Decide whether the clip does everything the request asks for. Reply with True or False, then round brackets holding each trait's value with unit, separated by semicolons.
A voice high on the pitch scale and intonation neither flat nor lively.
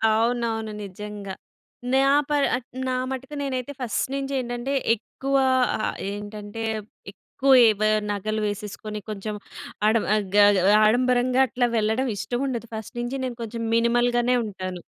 True (235 Hz; 3.2 semitones)